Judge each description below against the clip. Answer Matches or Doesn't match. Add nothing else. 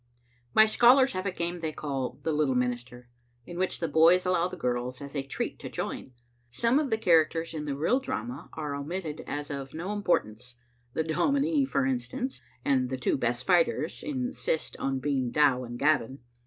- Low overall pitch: Doesn't match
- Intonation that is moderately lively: Doesn't match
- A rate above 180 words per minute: Matches